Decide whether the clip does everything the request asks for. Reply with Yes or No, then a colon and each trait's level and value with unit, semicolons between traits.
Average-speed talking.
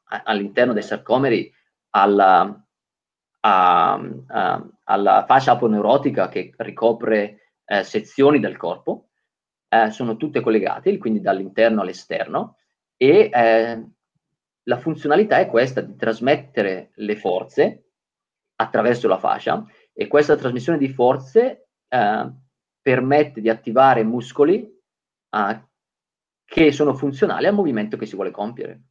No: slow, 110 wpm